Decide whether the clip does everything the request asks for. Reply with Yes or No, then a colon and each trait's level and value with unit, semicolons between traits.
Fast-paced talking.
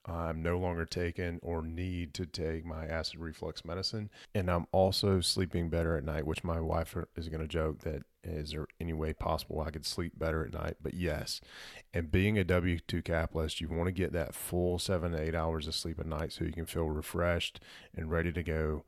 Yes: fast, 220 wpm